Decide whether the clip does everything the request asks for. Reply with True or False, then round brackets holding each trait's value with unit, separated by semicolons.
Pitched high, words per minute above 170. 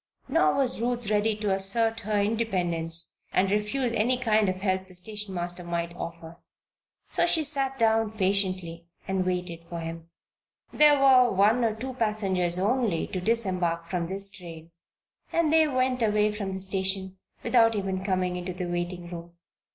False (195 Hz; 165 wpm)